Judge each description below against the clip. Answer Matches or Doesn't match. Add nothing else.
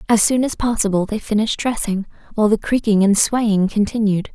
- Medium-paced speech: Matches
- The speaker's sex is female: Matches